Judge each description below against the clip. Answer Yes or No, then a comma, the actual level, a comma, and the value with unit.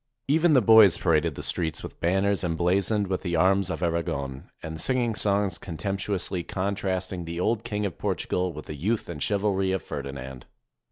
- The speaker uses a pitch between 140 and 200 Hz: No, very low, 95 Hz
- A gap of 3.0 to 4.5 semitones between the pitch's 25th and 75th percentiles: Yes, average, 3.5 semitones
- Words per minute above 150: Yes, average, 180 wpm